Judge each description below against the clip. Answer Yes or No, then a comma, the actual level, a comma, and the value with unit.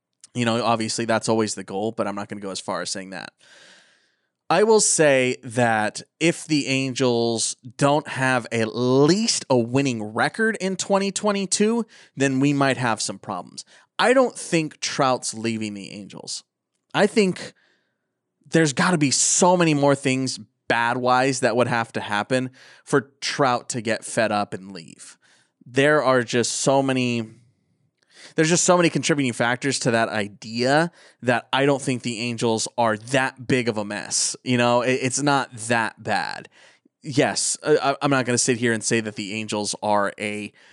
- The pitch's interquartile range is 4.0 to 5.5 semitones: Yes, average, 4.3 semitones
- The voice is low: Yes, low, 125 Hz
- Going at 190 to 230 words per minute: No, average, 175 wpm